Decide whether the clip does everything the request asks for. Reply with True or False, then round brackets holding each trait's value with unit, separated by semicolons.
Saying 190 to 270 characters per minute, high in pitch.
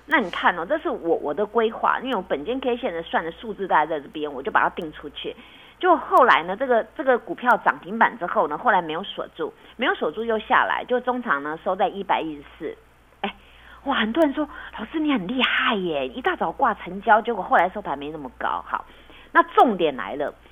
False (320 characters per minute; 230 Hz)